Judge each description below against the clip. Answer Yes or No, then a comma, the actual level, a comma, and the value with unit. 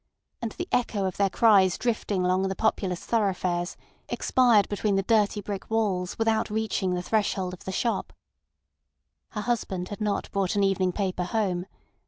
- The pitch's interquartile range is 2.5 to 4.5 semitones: Yes, average, 2.9 semitones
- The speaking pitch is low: No, high, 200 Hz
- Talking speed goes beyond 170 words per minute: No, average, 165 wpm